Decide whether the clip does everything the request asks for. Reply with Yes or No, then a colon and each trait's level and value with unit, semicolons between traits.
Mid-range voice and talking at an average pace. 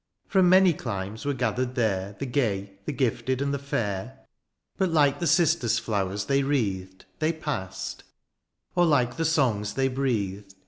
No: low, 130 Hz; average, 155 wpm